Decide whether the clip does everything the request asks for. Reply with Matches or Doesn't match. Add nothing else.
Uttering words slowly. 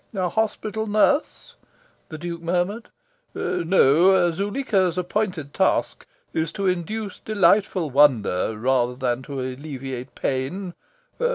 Matches